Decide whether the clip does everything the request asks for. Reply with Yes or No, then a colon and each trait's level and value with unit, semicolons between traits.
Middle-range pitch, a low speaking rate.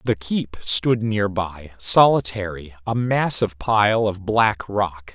No: low, 100 Hz; slow, 130 wpm